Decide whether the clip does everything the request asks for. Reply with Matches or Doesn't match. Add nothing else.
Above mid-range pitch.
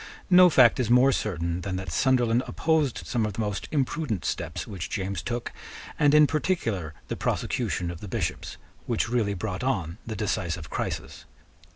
Doesn't match